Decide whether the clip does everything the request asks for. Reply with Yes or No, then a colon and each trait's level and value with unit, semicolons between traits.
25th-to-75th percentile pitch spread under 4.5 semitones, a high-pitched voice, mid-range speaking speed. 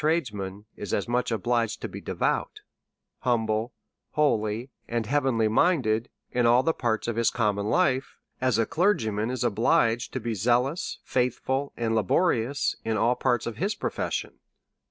No: average, 2.9 semitones; low, 120 Hz; average, 155 wpm